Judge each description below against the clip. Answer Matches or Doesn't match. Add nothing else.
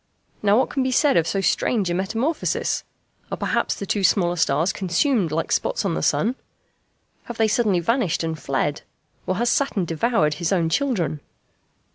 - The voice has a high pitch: Matches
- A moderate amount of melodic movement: Doesn't match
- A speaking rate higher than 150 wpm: Matches